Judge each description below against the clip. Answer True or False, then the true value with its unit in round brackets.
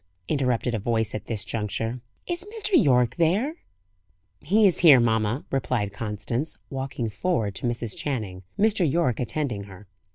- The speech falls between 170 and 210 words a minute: False (150 wpm)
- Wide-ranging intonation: True (6.6 semitones)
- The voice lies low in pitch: True (125 Hz)